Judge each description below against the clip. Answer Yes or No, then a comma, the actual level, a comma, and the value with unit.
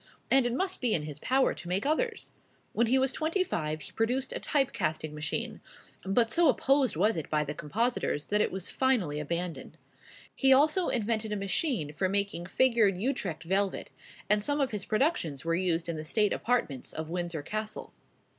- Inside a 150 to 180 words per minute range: No, average, 190 wpm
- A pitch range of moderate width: No, wide, 7.8 semitones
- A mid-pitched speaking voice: No, high, 205 Hz